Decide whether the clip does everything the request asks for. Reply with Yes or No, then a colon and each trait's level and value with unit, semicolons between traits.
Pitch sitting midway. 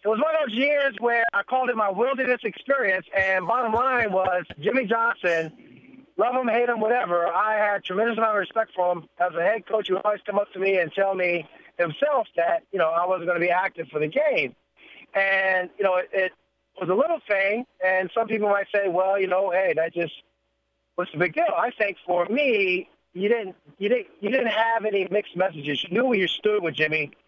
No: high, 200 Hz